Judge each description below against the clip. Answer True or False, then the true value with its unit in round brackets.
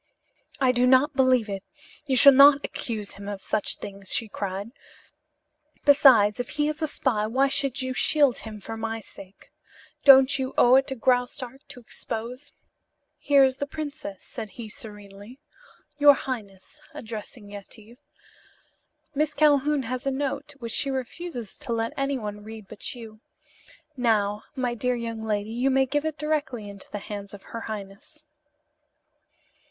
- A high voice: True (245 Hz)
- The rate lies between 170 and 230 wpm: False (160 wpm)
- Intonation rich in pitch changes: False (4.4 semitones)